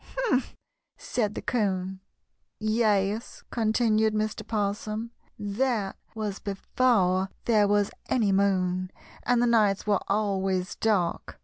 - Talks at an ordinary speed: No, slow, 110 wpm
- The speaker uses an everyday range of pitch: No, narrow, 2.3 semitones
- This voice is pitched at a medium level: No, high, 210 Hz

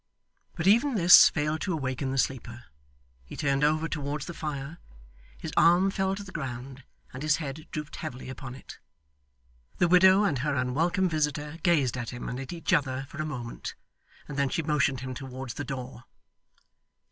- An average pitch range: Yes, average, 4.0 semitones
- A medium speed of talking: Yes, average, 180 wpm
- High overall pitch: No, medium, 150 Hz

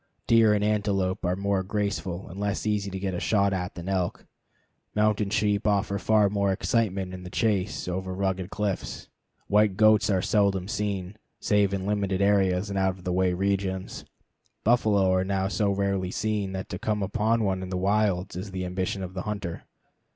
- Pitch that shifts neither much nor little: No, narrow, 1.8 semitones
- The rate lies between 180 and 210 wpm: Yes, average, 190 wpm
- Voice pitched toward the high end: No, low, 100 Hz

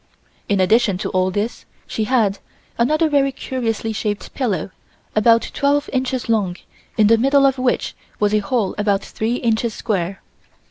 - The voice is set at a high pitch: Yes, high, 225 Hz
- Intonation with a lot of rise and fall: No, average, 4.0 semitones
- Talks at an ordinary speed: Yes, average, 155 wpm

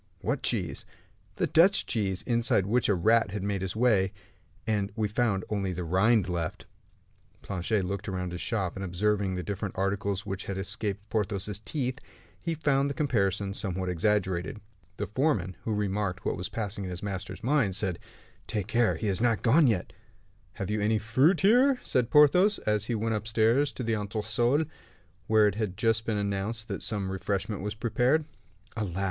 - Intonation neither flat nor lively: Yes, average, 3.1 semitones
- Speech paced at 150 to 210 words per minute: Yes, average, 180 wpm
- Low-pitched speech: Yes, low, 105 Hz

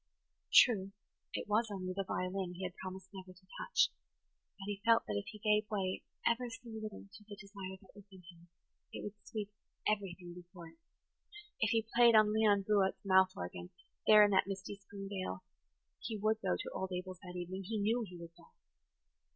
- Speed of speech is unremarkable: Yes, average, 195 wpm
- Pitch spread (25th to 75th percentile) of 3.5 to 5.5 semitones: No, narrow, 2.4 semitones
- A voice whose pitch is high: Yes, high, 195 Hz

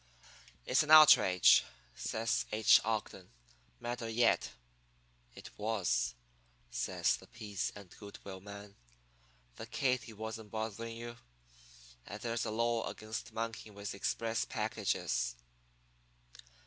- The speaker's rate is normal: No, slow, 110 wpm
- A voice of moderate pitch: No, low, 110 Hz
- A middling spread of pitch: No, narrow, 2.3 semitones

